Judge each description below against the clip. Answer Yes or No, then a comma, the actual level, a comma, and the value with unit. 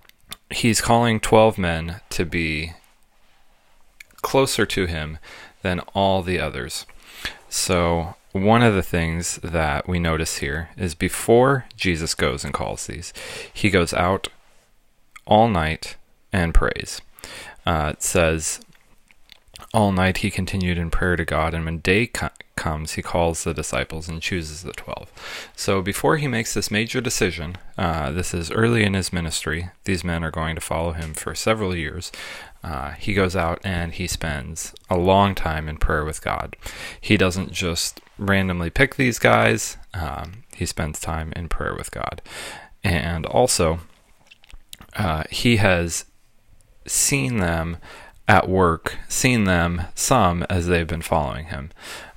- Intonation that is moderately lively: Yes, average, 3.7 semitones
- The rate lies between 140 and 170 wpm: Yes, average, 150 wpm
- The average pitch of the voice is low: Yes, very low, 90 Hz